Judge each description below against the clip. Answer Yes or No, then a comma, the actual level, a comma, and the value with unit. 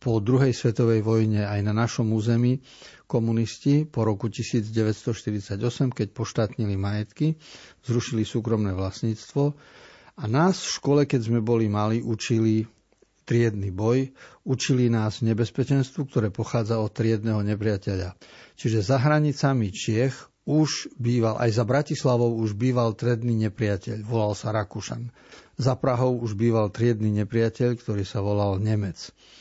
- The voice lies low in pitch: Yes, low, 115 Hz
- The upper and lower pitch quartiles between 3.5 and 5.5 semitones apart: No, average, 2.8 semitones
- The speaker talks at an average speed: Yes, average, 130 wpm